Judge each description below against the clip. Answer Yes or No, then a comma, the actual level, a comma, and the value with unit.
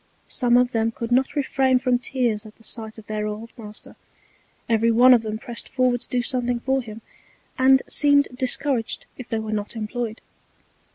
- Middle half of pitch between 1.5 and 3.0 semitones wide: Yes, narrow, 2.5 semitones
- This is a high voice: Yes, high, 240 Hz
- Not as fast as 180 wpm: No, average, 185 wpm